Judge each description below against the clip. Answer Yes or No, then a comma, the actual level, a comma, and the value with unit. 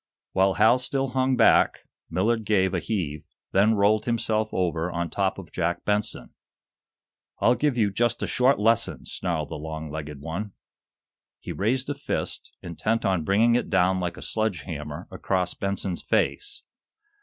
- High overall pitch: No, low, 100 Hz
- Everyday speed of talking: Yes, average, 160 wpm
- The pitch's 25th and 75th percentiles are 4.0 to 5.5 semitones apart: Yes, average, 4.7 semitones